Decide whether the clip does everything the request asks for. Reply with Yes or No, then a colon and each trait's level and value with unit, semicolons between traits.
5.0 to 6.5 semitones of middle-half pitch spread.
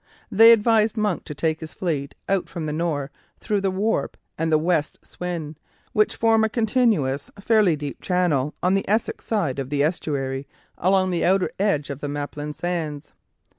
Yes: wide, 5.4 semitones